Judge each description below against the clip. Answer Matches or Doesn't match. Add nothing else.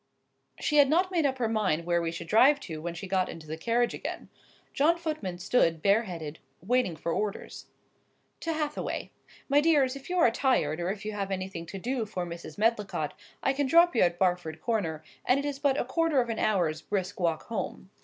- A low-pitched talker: Doesn't match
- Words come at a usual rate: Doesn't match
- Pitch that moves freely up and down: Matches